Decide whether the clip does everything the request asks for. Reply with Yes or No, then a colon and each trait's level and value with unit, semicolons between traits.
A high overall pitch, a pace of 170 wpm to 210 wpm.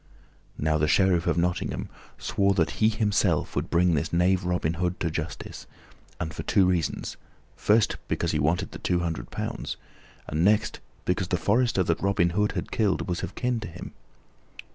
No: very low, 90 Hz; average, 180 wpm